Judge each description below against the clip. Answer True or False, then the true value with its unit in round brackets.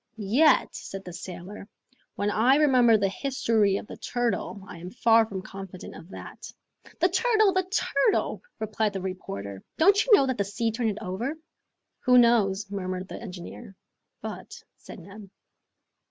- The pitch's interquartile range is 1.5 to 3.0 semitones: False (4.3 semitones)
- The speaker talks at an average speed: True (165 wpm)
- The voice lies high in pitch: True (210 Hz)